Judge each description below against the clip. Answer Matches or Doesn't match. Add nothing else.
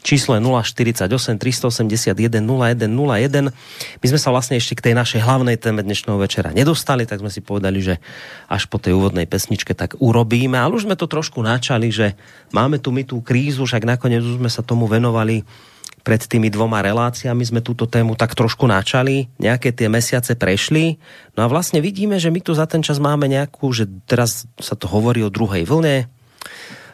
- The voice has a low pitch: Matches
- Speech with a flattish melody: Doesn't match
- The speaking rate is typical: Doesn't match